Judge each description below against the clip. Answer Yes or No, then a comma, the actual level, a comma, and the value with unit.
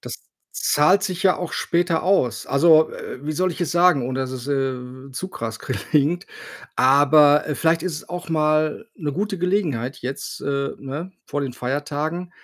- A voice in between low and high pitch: Yes, medium, 150 Hz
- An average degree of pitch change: Yes, average, 4.4 semitones